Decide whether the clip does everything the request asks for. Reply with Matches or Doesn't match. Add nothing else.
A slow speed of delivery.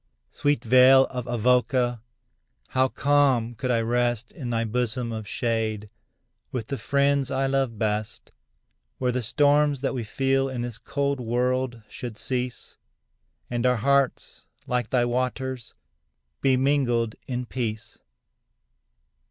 Matches